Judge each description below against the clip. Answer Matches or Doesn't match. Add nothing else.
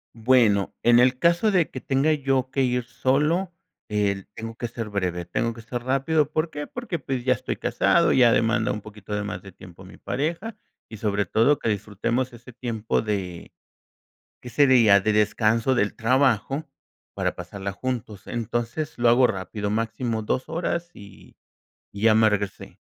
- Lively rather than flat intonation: Doesn't match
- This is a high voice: Doesn't match